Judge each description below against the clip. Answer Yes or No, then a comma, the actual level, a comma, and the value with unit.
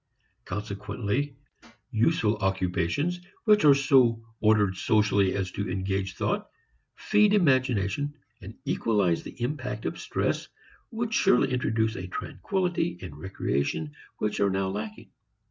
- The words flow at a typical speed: No, slow, 120 wpm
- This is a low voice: Yes, low, 105 Hz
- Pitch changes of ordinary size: No, wide, 6.3 semitones